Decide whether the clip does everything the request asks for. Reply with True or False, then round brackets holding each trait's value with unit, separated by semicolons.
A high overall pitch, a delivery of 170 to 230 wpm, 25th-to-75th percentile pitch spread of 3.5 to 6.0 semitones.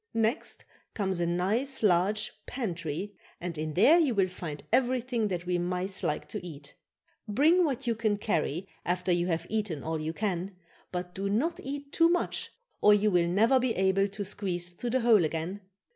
True (195 Hz; 185 wpm; 4.7 semitones)